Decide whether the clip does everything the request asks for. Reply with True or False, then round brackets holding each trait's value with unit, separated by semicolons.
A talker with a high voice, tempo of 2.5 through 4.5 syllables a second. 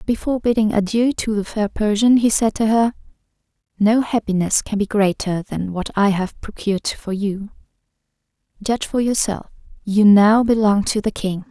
False (210 Hz; 5.0 syllables/s)